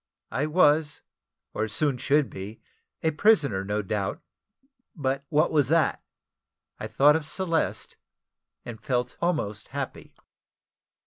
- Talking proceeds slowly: Yes, slow, 120 wpm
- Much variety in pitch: Yes, wide, 6.0 semitones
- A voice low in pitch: No, medium, 145 Hz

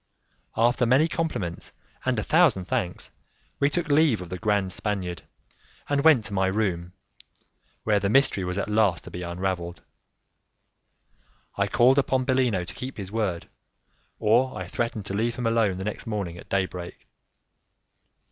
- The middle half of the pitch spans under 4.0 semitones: No, wide, 5.4 semitones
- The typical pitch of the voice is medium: No, low, 105 Hz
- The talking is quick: No, average, 160 wpm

